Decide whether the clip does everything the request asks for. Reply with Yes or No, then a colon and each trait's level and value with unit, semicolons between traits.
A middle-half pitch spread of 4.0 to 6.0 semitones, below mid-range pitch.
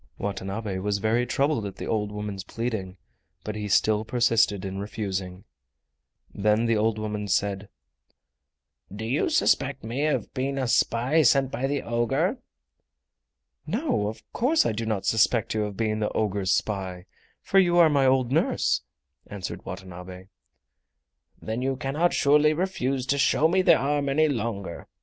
Yes: average, 5.1 semitones; low, 110 Hz